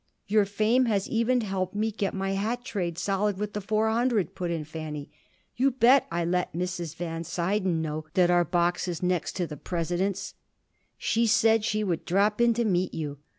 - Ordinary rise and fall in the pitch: Yes, average, 3.8 semitones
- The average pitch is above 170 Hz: Yes, high, 190 Hz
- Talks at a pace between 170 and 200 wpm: Yes, average, 195 wpm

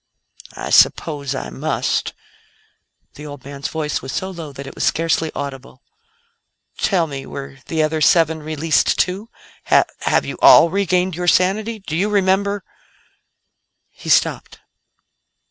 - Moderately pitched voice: Yes, medium, 160 Hz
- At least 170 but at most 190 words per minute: No, average, 145 wpm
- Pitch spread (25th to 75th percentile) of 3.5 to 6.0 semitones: Yes, average, 4.7 semitones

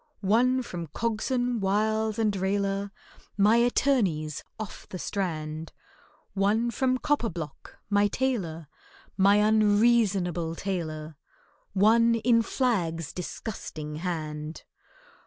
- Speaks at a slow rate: Yes, slow, 95 wpm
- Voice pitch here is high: Yes, high, 200 Hz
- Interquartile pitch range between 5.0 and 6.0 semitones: Yes, wide, 5.5 semitones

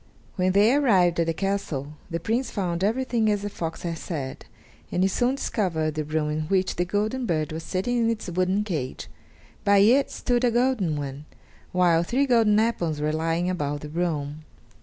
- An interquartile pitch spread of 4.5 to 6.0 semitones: Yes, wide, 5.5 semitones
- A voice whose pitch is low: No, medium, 185 Hz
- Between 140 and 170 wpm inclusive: No, average, 190 wpm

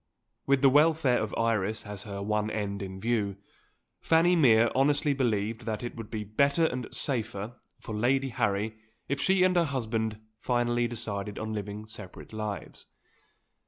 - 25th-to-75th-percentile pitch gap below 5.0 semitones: Yes, average, 4.1 semitones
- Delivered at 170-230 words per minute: No, average, 160 wpm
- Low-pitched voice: Yes, low, 115 Hz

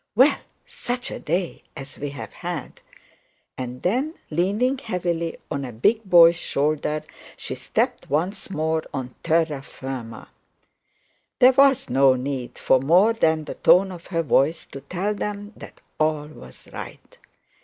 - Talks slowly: No, average, 145 wpm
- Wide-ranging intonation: Yes, wide, 6.4 semitones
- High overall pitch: No, medium, 165 Hz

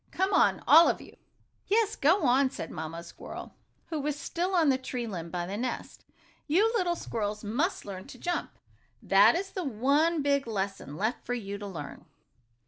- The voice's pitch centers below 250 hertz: No, very high, 255 Hz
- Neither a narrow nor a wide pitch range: No, wide, 8.7 semitones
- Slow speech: No, average, 185 wpm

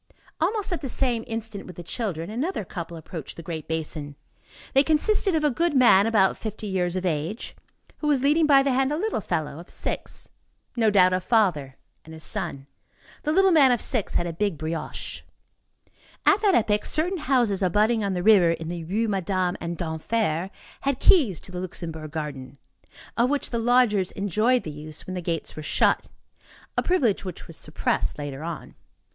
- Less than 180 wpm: No, average, 185 wpm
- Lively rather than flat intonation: Yes, wide, 7.4 semitones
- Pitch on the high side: Yes, high, 200 Hz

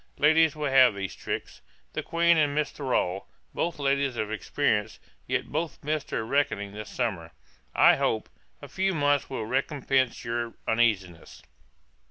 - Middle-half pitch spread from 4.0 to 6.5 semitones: Yes, average, 5.2 semitones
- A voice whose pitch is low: Yes, low, 130 Hz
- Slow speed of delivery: No, average, 150 wpm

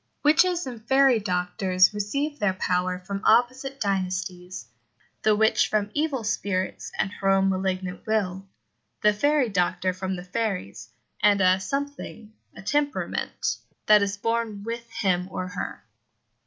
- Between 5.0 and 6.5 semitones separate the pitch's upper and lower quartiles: No, average, 3.9 semitones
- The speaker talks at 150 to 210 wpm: No, average, 140 wpm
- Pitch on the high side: Yes, high, 200 Hz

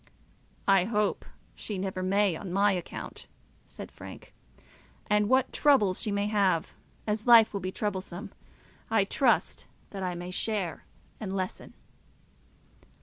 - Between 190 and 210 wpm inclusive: No, slow, 135 wpm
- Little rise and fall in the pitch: Yes, narrow, 2.2 semitones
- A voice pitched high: Yes, high, 200 Hz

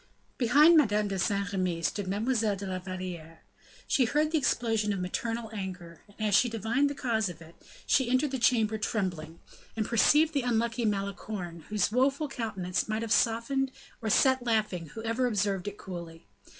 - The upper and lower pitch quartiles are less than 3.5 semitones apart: No, average, 4.5 semitones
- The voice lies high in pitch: Yes, high, 215 Hz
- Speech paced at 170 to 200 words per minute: Yes, average, 175 wpm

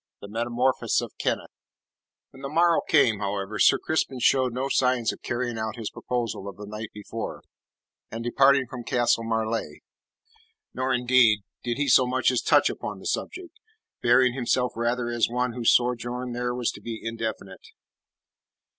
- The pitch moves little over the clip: Yes, narrow, 2.1 semitones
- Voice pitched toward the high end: No, low, 120 Hz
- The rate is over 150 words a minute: Yes, average, 165 wpm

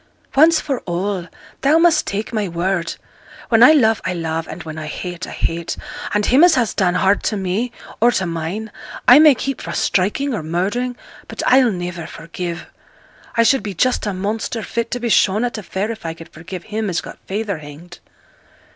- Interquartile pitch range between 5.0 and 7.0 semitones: Yes, average, 5.3 semitones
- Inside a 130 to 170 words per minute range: No, average, 200 wpm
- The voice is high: Yes, high, 200 Hz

